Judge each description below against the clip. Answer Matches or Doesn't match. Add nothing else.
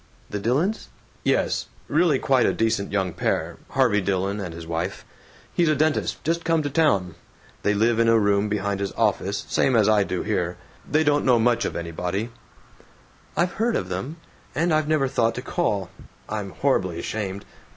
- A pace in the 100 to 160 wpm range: Doesn't match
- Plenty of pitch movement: Matches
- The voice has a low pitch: Matches